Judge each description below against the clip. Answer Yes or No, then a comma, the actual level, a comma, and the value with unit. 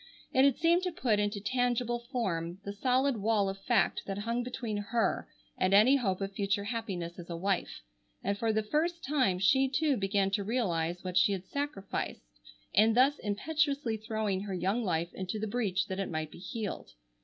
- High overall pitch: Yes, high, 210 Hz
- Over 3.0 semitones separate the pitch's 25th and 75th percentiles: Yes, average, 4.3 semitones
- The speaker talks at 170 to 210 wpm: Yes, average, 190 wpm